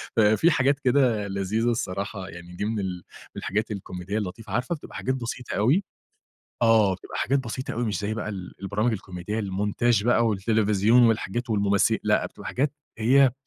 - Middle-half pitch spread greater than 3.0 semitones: Yes, average, 3.4 semitones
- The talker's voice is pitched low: Yes, low, 110 Hz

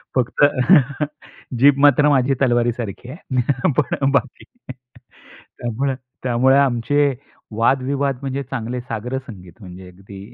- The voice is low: Yes, low, 125 Hz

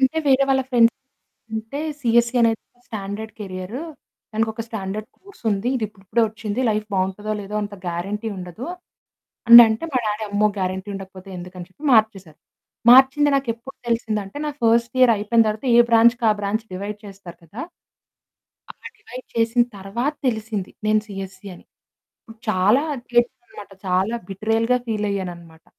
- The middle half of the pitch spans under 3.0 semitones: No, average, 3.3 semitones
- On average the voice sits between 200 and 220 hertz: Yes, high, 215 Hz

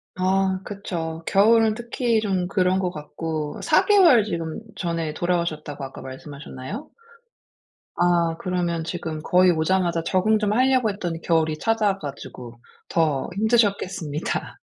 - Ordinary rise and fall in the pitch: Yes, average, 4.2 semitones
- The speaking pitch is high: No, medium, 180 Hz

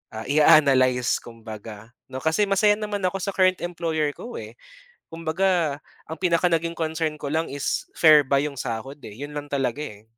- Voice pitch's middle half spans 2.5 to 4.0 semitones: No, average, 4.6 semitones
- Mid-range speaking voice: Yes, medium, 155 Hz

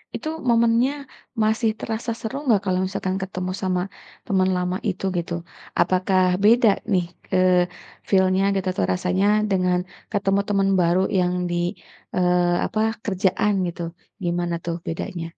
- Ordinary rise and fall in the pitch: No, narrow, 2.2 semitones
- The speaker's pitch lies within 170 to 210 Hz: Yes, medium, 185 Hz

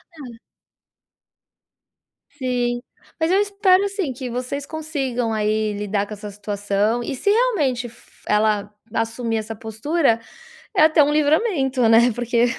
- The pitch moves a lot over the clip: Yes, wide, 5.7 semitones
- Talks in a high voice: Yes, high, 245 Hz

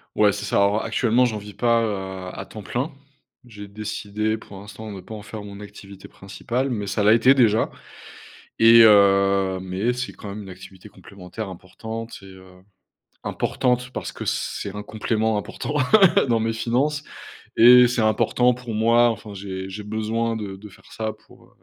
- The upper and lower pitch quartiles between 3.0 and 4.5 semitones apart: No, narrow, 2.6 semitones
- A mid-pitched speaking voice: No, low, 105 Hz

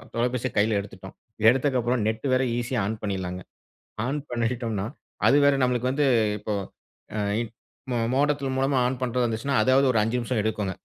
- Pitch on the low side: Yes, low, 120 Hz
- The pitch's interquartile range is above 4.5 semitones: No, average, 3.1 semitones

